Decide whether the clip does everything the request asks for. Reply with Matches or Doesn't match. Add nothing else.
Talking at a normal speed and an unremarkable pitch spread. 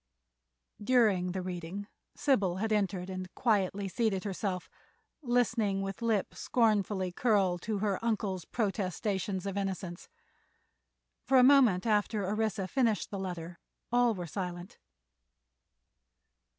Doesn't match